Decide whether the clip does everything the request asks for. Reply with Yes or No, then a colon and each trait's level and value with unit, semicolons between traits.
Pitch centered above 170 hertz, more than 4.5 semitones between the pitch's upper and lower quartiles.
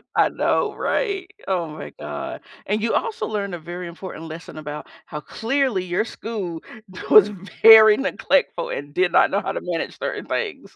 Yes: high, 190 Hz; average, 5.1 semitones